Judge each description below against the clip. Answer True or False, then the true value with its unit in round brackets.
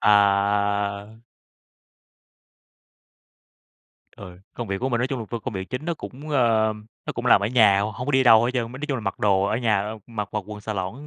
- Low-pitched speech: True (110 Hz)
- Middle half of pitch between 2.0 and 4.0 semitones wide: True (3.6 semitones)